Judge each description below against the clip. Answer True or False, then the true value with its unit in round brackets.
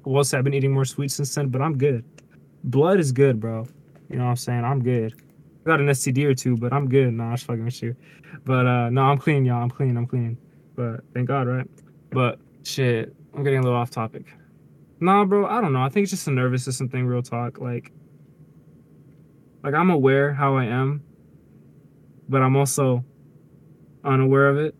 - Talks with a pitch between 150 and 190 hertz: False (135 Hz)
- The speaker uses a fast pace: True (215 wpm)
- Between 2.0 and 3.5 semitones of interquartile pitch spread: True (2.7 semitones)